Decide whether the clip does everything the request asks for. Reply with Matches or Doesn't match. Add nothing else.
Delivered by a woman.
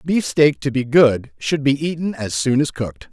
Doesn't match